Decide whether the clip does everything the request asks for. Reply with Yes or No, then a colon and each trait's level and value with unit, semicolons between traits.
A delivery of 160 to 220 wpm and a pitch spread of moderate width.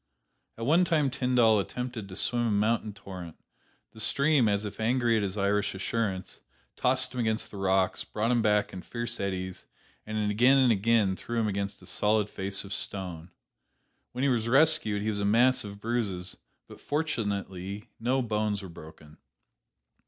Yes: average, 175 wpm; average, 3.4 semitones